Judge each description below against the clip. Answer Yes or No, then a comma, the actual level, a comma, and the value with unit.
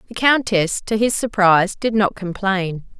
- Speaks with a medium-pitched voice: No, high, 200 Hz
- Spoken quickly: No, average, 160 wpm